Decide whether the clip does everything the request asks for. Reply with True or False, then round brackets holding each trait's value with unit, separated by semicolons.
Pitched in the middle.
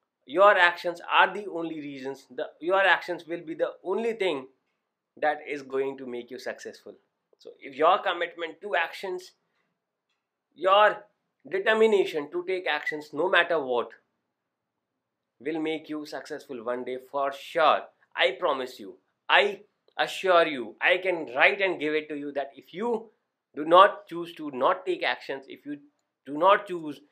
True (170 Hz)